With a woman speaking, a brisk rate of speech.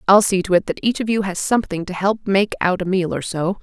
Yes: female; fast, 300 wpm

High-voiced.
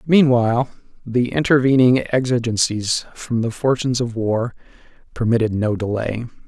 No: low, 120 Hz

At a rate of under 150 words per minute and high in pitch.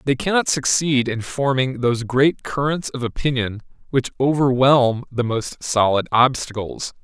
No: slow, 135 wpm; low, 130 Hz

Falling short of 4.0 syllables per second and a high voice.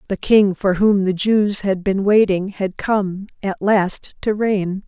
Yes: 3.6 syllables/s; high, 195 Hz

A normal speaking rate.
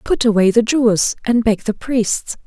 Yes: average, 195 wpm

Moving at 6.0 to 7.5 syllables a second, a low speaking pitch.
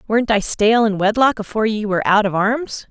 No: 6.3 syllables/s; high, 215 Hz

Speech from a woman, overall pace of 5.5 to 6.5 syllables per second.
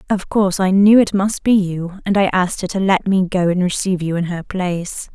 Yes: female; 5.7 syllables/s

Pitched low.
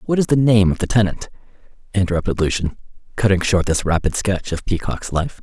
Yes: very low, 95 Hz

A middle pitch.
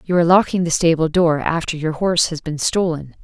Yes: medium, 165 Hz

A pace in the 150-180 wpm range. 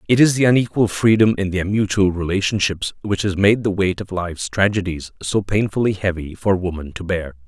No: average, 195 wpm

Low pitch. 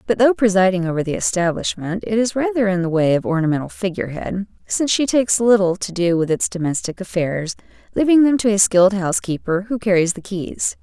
No: high, 195 Hz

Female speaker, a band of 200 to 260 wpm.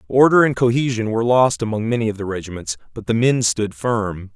No: male; fast, 205 wpm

